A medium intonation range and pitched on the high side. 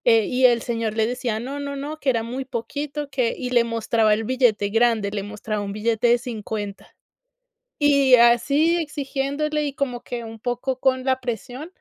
Yes: average, 3.4 semitones; high, 245 Hz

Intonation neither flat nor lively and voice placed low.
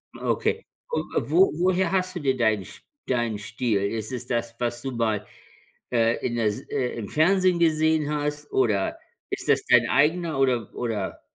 No: wide, 5.7 semitones; low, 125 Hz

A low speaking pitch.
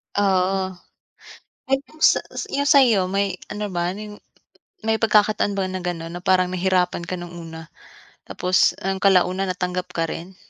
No: medium, 185 Hz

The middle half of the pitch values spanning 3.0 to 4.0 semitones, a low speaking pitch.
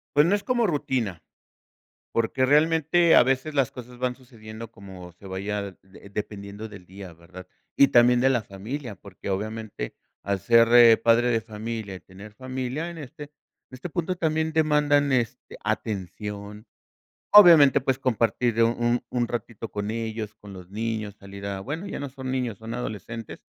No: average, 4.6 semitones; low, 115 Hz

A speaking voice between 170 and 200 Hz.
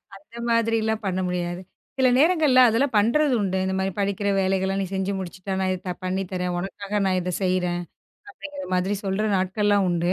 Yes: high, 195 Hz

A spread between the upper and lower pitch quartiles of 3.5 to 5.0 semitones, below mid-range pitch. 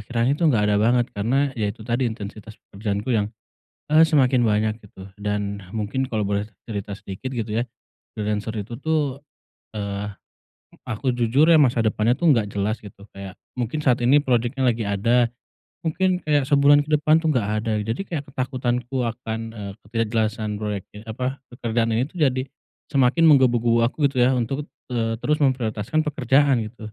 Yes: average, 4.0 semitones; low, 120 Hz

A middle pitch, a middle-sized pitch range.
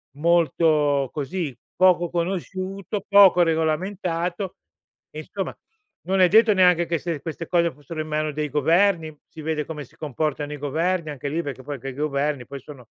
Yes: medium, 160 Hz; average, 3.3 semitones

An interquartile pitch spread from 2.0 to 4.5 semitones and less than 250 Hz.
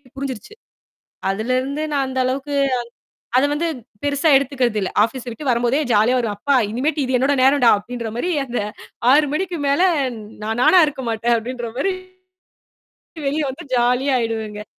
No: average, 3.3 semitones; very high, 255 Hz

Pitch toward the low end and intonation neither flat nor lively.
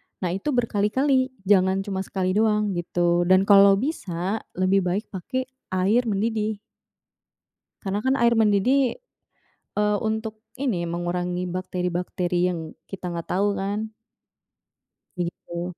No: high, 195 Hz; average, 3.3 semitones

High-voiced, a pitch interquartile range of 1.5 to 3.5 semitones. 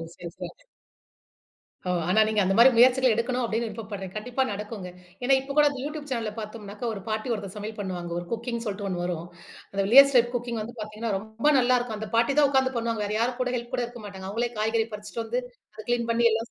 Yes: high, 225 Hz; average, 2.8 semitones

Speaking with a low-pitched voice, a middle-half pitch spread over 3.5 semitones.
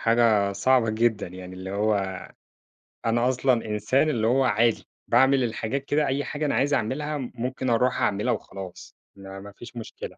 Yes: low, 115 Hz; average, 3.9 semitones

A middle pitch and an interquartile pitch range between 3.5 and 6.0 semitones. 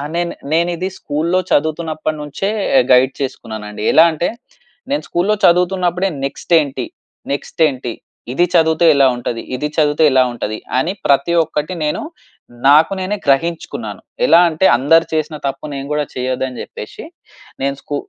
Yes: medium, 150 Hz; average, 4.0 semitones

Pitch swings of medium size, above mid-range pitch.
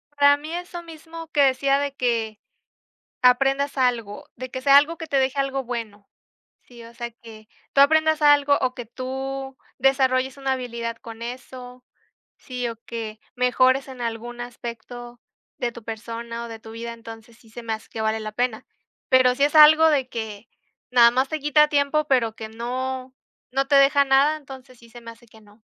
Yes: average, 3.0 semitones; very high, 255 Hz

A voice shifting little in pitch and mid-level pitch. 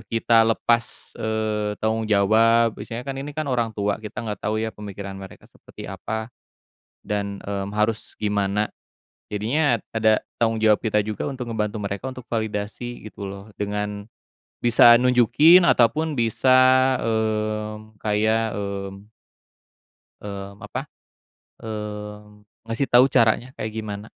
No: narrow, 1.9 semitones; low, 110 Hz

